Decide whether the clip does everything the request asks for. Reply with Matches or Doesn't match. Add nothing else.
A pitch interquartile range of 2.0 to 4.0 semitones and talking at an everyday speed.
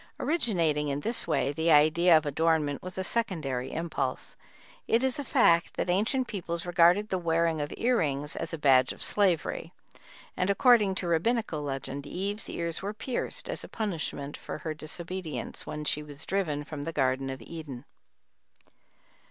Doesn't match